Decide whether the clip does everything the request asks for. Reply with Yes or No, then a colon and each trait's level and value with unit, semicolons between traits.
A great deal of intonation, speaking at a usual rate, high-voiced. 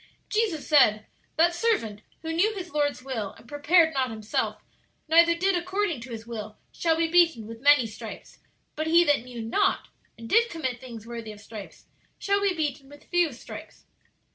Yes: wide, 6.9 semitones; average, 180 wpm; very high, 290 Hz